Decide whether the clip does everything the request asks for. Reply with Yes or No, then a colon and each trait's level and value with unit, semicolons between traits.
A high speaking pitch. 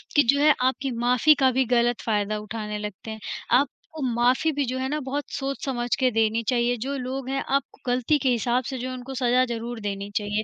Yes: very high, 250 Hz